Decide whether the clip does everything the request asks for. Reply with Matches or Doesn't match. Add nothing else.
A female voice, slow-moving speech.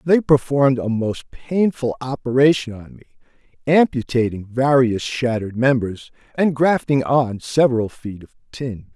Doesn't match